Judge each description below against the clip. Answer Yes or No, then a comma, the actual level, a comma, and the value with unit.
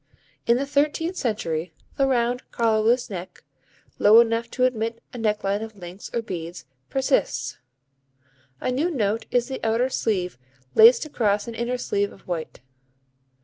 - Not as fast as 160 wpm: Yes, average, 145 wpm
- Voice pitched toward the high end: Yes, high, 230 Hz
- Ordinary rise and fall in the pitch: Yes, average, 3.7 semitones